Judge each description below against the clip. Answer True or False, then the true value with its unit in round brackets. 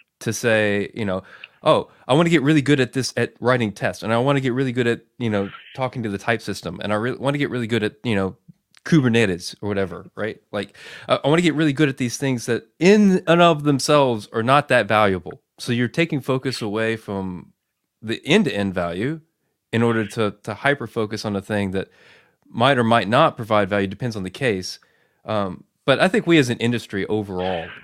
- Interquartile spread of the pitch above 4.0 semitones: True (5.0 semitones)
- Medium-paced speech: False (225 wpm)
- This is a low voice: True (115 Hz)